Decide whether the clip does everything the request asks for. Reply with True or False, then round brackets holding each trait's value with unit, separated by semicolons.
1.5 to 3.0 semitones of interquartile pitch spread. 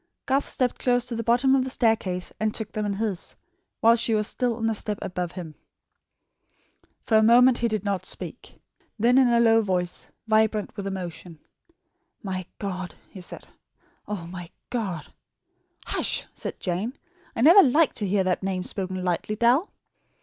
False (4.1 semitones)